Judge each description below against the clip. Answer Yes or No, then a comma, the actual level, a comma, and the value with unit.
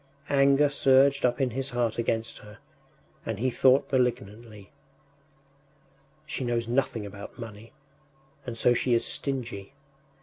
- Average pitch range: Yes, average, 3.0 semitones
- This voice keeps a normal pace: No, slow, 130 wpm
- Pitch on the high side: No, low, 120 Hz